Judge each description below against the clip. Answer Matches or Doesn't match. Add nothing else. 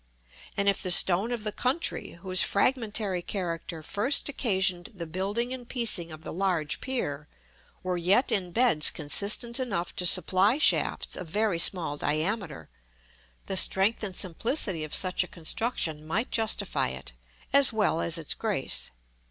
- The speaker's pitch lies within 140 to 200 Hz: Matches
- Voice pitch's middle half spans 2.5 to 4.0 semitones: Doesn't match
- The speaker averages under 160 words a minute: Matches